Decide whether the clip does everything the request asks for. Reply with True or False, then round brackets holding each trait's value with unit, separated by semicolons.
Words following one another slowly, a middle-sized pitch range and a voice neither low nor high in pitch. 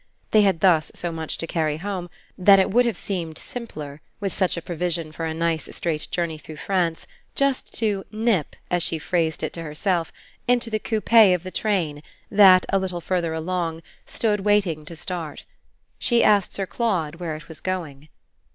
False (185 wpm; 3.7 semitones; 175 Hz)